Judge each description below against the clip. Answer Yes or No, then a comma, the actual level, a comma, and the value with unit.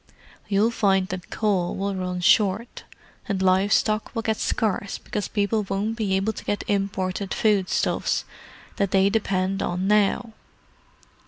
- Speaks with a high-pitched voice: Yes, high, 200 Hz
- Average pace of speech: Yes, average, 150 wpm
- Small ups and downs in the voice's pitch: Yes, narrow, 2.0 semitones